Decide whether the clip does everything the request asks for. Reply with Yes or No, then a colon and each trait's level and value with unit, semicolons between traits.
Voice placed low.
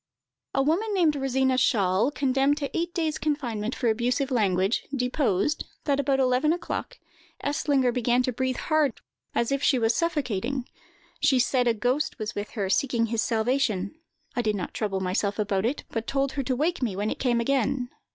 No: very high, 255 Hz